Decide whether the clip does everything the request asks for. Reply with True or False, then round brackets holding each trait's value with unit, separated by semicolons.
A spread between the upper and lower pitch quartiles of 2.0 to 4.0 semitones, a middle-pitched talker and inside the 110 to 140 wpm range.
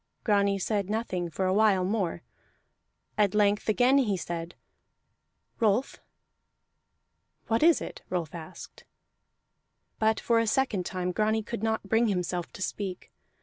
False (3.4 semitones; 205 Hz; 135 wpm)